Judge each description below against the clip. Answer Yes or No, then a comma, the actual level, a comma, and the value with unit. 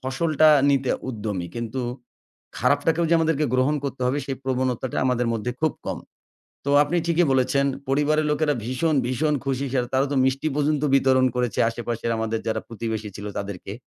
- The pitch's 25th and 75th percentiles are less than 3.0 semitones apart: No, average, 3.8 semitones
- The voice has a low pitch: Yes, low, 130 Hz